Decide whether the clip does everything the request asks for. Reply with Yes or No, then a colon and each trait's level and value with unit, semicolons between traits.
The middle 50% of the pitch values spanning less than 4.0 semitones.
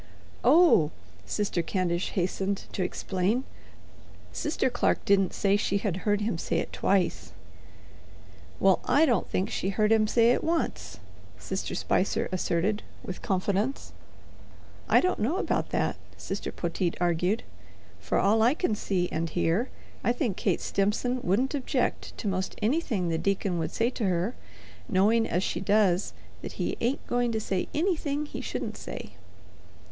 No: average, 4.7 semitones